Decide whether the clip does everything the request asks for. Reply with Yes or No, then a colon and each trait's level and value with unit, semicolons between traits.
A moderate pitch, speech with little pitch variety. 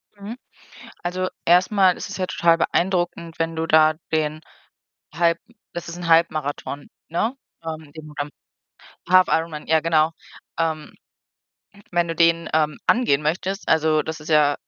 Yes: medium, 165 Hz; narrow, 2.0 semitones